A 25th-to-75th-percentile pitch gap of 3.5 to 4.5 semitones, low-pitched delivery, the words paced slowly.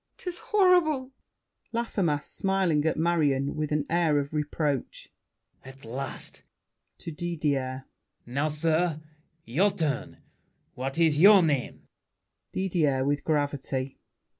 No: average, 3.8 semitones; medium, 150 Hz; slow, 110 wpm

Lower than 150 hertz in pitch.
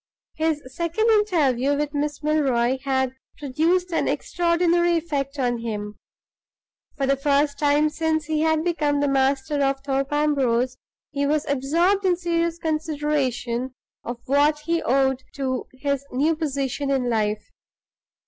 No: very high, 285 Hz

